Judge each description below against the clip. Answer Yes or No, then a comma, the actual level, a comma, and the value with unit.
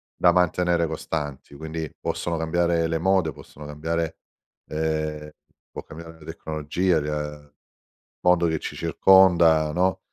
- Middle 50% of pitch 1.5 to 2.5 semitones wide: Yes, narrow, 2.1 semitones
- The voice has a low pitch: Yes, very low, 80 Hz